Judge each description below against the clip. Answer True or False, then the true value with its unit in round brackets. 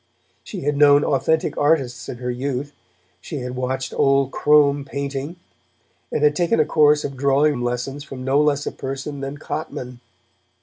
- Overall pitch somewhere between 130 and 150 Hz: True (140 Hz)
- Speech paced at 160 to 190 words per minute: True (165 wpm)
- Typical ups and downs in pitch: False (1.9 semitones)